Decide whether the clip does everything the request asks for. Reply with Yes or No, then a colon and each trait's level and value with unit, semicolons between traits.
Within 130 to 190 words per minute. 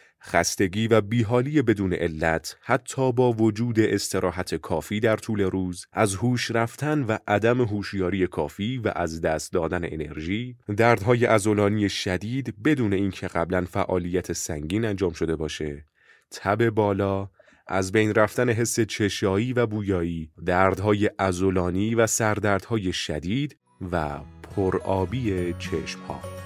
No: average, 120 wpm